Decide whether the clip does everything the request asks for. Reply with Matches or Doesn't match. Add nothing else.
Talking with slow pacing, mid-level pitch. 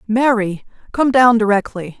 Doesn't match